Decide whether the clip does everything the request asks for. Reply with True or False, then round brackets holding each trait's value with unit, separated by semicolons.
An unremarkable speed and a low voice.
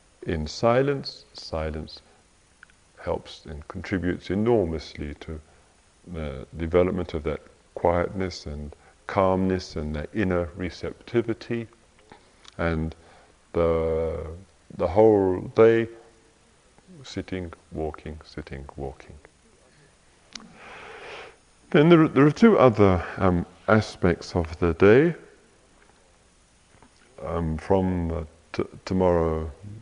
False (90 wpm; 90 Hz)